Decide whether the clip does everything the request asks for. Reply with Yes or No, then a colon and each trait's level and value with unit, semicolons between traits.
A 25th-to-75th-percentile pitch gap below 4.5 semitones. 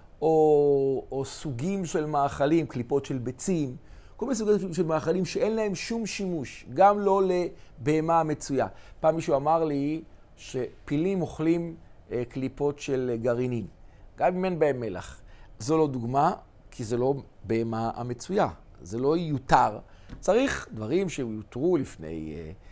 No: wide, 5.5 semitones